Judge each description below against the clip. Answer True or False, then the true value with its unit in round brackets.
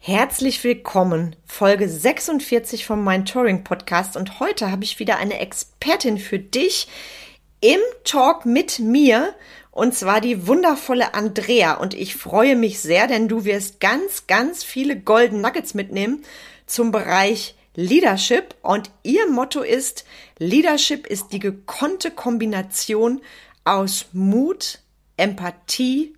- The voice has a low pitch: False (230 Hz)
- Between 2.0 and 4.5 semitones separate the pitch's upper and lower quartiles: False (5.3 semitones)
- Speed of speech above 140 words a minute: False (125 wpm)